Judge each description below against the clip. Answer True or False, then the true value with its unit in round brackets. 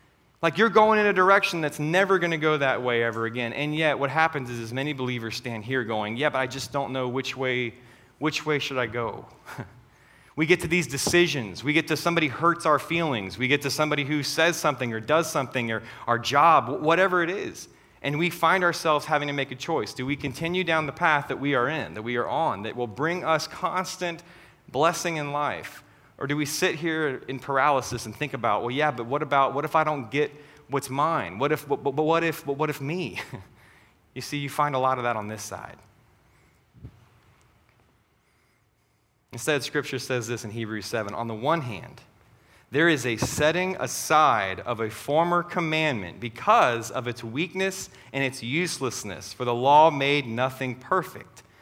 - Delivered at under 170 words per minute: False (200 wpm)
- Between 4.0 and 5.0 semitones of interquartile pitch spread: True (4.6 semitones)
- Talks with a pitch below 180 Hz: True (140 Hz)